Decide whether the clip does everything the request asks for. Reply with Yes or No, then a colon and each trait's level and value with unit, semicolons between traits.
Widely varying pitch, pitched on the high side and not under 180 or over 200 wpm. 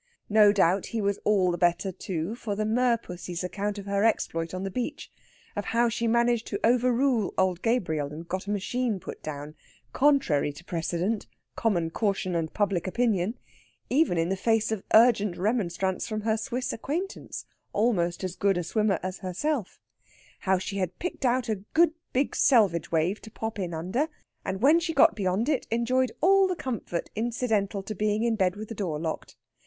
No: average, 4.5 semitones; high, 205 Hz; average, 185 wpm